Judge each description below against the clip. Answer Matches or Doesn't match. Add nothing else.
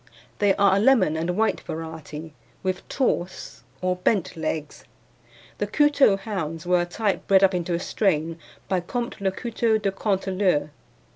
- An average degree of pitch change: Matches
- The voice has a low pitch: Doesn't match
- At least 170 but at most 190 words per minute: Doesn't match